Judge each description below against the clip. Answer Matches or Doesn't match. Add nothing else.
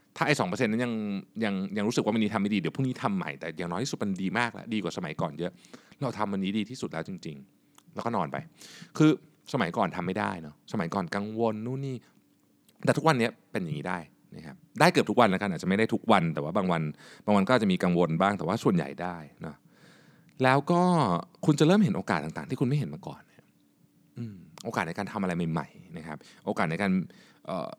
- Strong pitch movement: Matches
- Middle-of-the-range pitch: Doesn't match